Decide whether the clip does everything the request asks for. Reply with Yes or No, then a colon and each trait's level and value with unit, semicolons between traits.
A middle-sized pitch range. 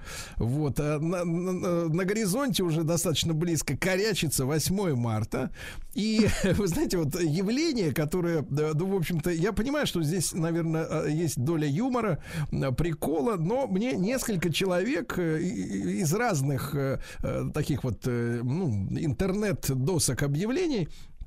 Yes: average, 4.4 semitones